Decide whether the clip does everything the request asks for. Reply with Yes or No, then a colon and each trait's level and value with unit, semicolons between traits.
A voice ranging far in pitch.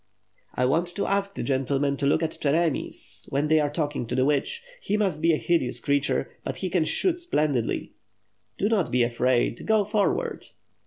Yes: wide, 5.7 semitones